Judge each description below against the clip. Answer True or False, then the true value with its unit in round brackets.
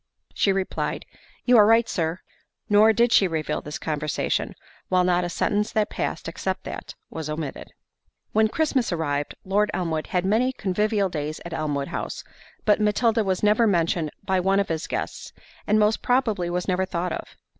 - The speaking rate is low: False (175 wpm)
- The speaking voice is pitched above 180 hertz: True (190 Hz)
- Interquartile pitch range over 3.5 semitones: True (4.4 semitones)